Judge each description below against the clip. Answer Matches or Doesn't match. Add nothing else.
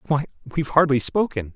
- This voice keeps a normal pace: Matches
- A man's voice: Matches